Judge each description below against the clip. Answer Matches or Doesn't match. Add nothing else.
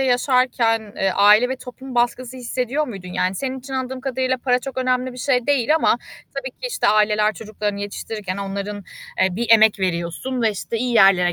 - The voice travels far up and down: Doesn't match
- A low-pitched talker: Doesn't match